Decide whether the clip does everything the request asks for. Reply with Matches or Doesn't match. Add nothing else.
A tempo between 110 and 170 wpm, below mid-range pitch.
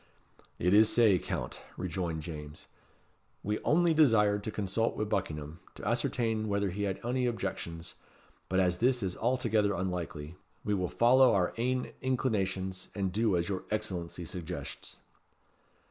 Matches